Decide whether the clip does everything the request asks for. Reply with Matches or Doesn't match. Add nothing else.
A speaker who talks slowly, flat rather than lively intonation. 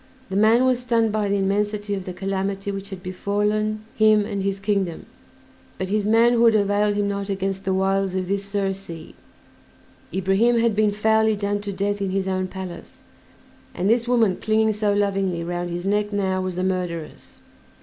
Doesn't match